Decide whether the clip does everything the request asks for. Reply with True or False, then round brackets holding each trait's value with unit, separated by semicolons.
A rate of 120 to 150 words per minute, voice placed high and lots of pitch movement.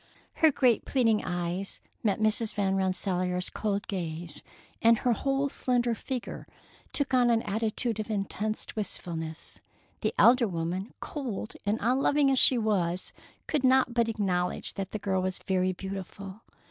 False (145 wpm; 210 Hz; 4.4 semitones)